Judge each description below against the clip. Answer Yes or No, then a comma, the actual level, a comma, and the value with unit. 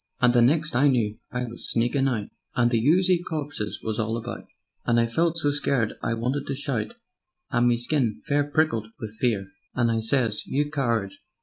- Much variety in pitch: No, average, 4.1 semitones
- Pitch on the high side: No, low, 120 Hz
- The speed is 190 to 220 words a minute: Yes, average, 195 wpm